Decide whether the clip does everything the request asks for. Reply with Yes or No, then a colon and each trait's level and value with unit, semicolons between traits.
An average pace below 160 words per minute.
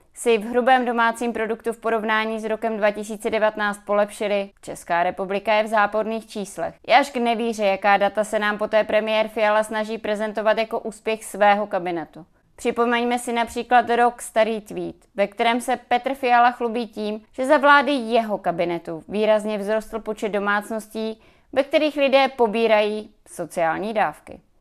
Yes: average, 150 wpm